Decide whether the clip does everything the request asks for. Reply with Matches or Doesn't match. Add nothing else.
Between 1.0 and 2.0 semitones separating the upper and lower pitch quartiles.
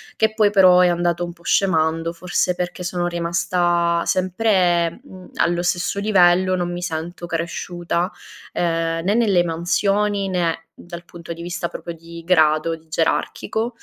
Matches